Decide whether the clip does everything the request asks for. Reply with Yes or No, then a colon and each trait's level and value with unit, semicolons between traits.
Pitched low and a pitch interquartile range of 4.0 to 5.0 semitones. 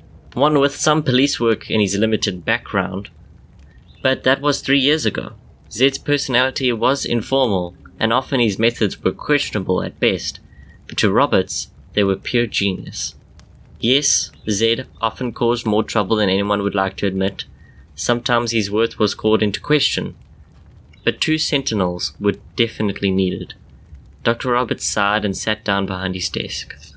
Yes: low, 110 Hz; average, 4.3 semitones